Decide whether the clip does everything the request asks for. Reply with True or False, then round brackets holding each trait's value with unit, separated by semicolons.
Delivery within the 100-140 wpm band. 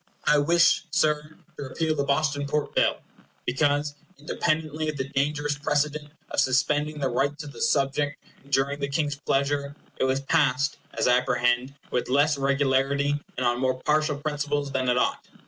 False (160 wpm)